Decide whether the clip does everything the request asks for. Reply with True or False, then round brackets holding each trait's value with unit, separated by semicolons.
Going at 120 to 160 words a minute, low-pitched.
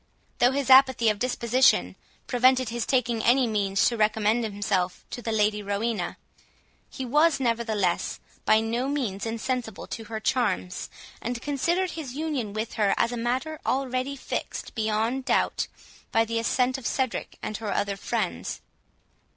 False (150 wpm; 235 Hz)